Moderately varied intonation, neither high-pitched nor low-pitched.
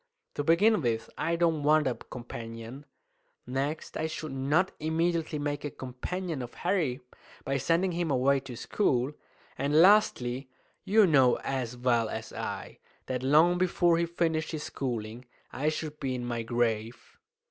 Yes: average, 5.0 semitones; medium, 145 Hz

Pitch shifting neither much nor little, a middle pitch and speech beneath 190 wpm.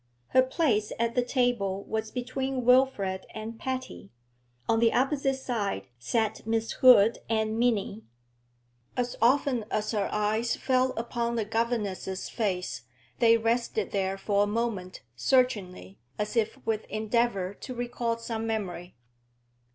No: average, 3.1 semitones; high, 225 Hz; slow, 135 wpm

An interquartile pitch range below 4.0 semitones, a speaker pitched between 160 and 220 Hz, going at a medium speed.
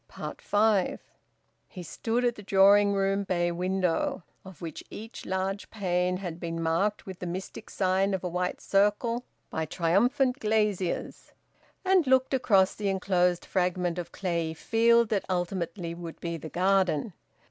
Yes: average, 2.8 semitones; high, 190 Hz; average, 145 wpm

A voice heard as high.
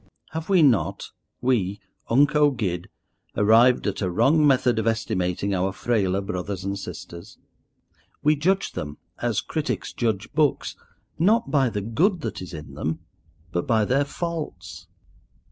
No: low, 110 Hz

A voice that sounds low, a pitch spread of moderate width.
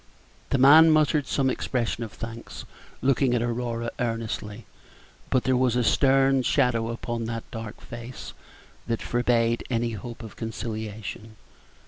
No: low, 120 Hz; narrow, 2.1 semitones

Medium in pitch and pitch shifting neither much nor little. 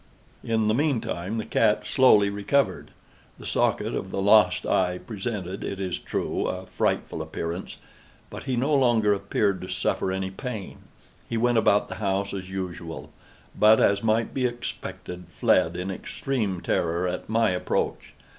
No: low, 100 Hz; average, 3.5 semitones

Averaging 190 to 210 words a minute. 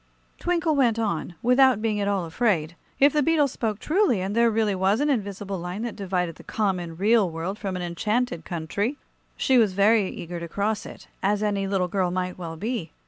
Yes: average, 200 wpm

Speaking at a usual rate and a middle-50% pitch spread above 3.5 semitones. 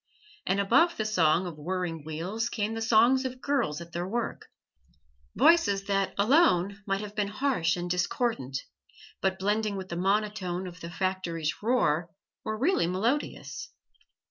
Yes: average, 150 wpm; average, 4.3 semitones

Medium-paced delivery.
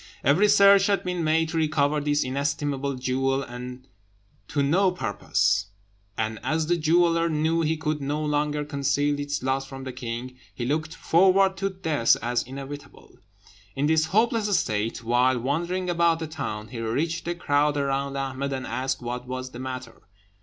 Yes: average, 165 wpm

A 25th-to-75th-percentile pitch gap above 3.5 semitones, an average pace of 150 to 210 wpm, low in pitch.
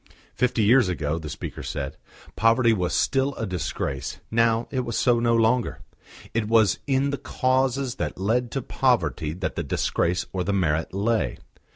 Yes: wide, 5.6 semitones; average, 170 wpm; low, 115 Hz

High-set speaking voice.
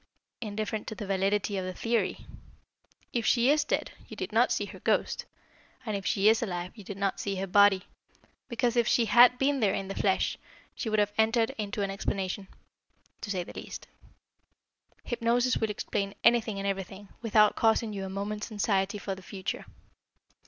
Yes: high, 205 Hz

